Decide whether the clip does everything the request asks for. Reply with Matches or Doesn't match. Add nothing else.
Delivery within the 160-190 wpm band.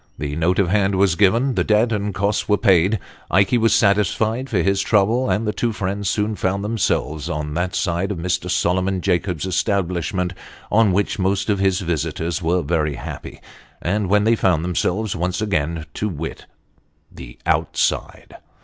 Matches